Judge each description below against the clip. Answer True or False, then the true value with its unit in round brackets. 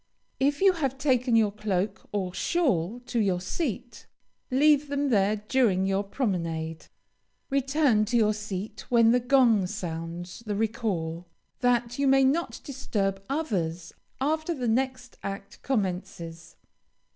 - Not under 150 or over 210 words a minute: False (135 wpm)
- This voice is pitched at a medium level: False (225 Hz)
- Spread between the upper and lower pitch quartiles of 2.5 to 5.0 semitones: False (5.6 semitones)